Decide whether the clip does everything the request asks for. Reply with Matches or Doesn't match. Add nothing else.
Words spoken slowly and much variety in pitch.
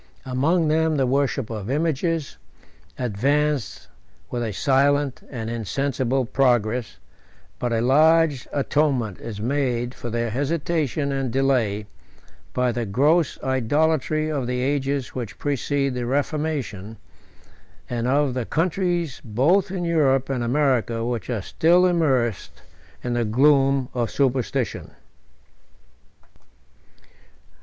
Doesn't match